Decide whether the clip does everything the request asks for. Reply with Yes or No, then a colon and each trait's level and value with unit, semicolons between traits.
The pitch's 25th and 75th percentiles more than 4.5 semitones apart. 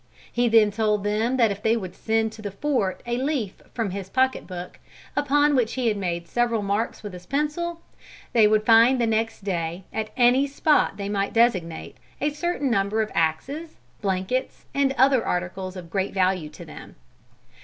Yes: average, 5.0 semitones